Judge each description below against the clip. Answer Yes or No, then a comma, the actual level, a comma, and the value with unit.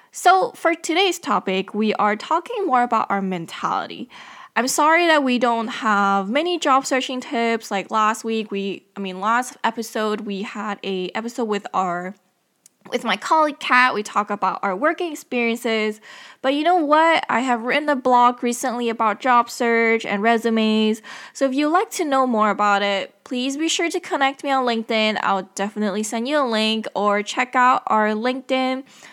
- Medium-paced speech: Yes, average, 180 wpm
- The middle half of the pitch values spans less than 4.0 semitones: No, average, 4.4 semitones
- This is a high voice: Yes, high, 235 Hz